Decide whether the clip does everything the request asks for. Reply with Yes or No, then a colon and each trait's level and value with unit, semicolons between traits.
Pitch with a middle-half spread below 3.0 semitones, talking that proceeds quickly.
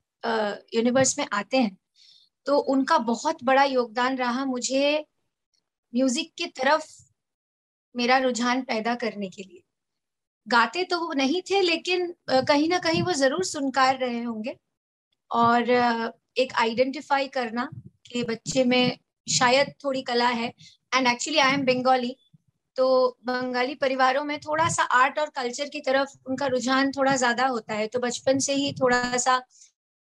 No: narrow, 2.4 semitones; average, 150 wpm